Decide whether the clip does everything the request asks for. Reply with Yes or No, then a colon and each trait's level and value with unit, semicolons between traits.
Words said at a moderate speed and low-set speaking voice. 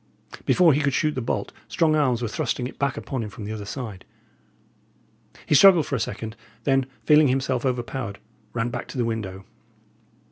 Yes: average, 185 wpm; low, 125 Hz